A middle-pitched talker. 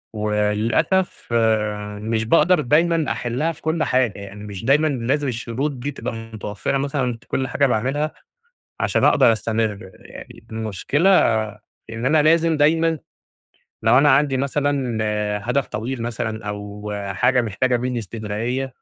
No: low, 120 Hz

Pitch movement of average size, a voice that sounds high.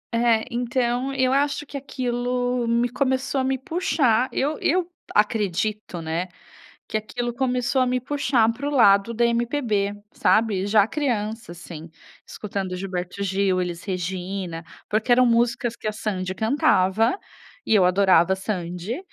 Yes: average, 4.5 semitones; high, 225 Hz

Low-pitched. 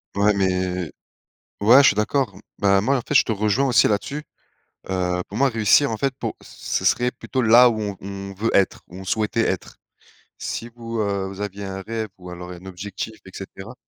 Yes: low, 100 Hz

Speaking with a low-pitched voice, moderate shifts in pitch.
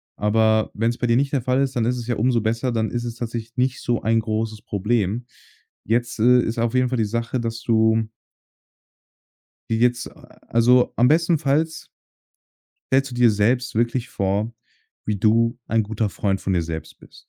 No: low, 115 Hz; narrow, 2.0 semitones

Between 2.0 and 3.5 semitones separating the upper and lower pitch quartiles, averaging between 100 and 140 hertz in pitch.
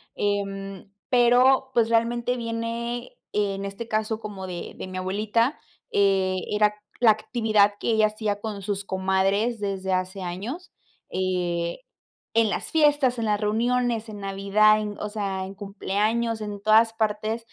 No: average, 2.7 semitones; high, 210 Hz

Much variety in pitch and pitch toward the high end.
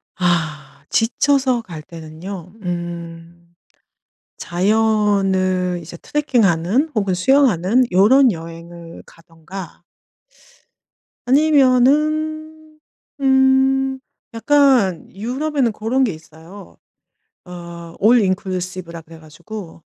Yes: wide, 7.5 semitones; high, 195 Hz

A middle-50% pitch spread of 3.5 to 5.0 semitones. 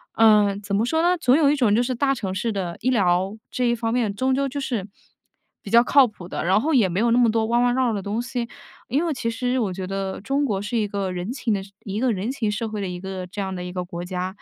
Yes: average, 4.4 semitones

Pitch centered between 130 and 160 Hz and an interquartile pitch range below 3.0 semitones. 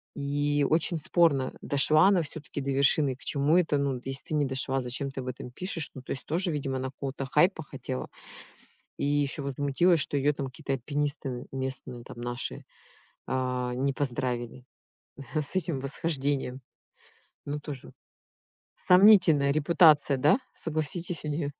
Yes: medium, 140 Hz; narrow, 2.6 semitones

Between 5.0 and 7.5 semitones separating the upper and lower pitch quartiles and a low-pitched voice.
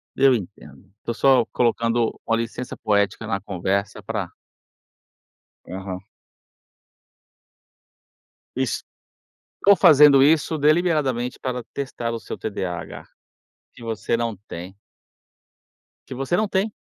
Yes: average, 5.3 semitones; low, 115 Hz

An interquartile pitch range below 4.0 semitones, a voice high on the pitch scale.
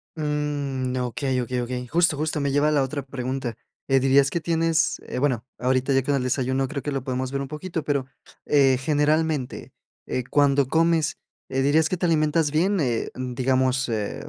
No: average, 2.8 semitones; medium, 140 Hz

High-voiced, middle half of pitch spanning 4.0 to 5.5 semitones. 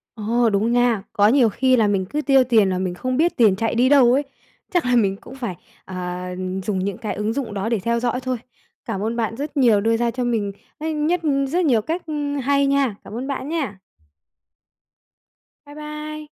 Yes: high, 240 Hz; average, 5.0 semitones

